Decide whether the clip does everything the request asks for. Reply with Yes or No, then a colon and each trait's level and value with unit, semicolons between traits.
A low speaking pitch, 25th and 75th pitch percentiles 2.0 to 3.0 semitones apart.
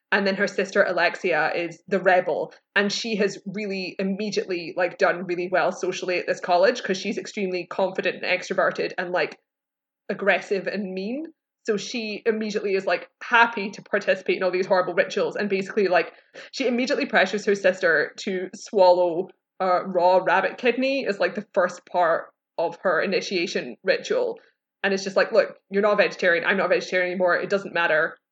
No: high, 195 Hz; narrow, 2.5 semitones